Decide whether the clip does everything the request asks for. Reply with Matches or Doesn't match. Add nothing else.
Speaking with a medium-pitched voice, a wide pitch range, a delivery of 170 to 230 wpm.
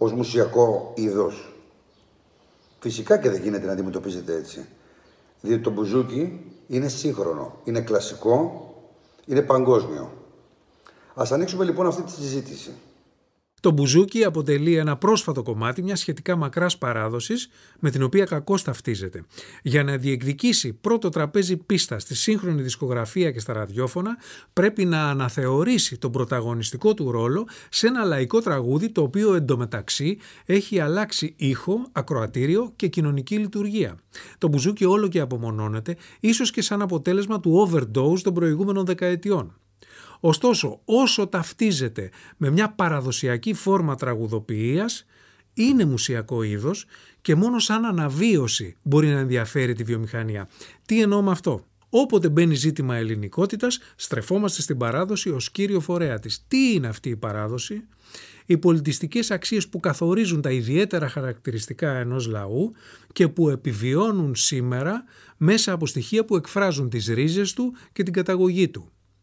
Doesn't match